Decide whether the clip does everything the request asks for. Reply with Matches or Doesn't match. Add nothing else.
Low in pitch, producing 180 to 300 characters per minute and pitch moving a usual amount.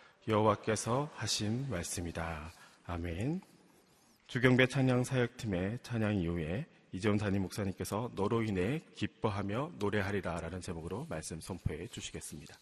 Doesn't match